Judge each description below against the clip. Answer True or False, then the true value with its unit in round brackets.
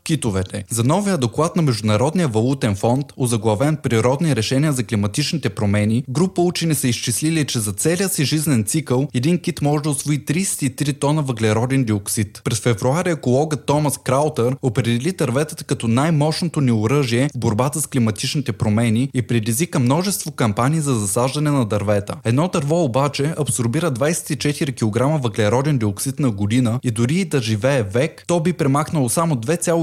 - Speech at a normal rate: True (155 wpm)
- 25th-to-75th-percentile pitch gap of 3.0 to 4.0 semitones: False (4.6 semitones)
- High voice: False (135 Hz)